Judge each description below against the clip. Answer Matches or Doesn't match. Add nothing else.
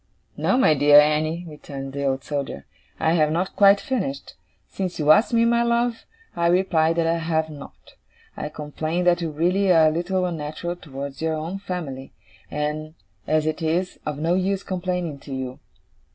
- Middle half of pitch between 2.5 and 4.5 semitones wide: Matches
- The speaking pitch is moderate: Matches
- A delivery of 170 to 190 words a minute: Matches